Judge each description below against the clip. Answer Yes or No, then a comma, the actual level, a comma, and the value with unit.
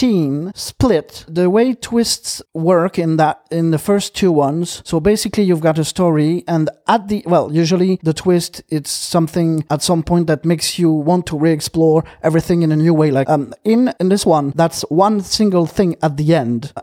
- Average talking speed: Yes, average, 195 wpm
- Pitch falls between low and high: Yes, medium, 170 Hz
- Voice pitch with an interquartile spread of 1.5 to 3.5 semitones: Yes, narrow, 2.6 semitones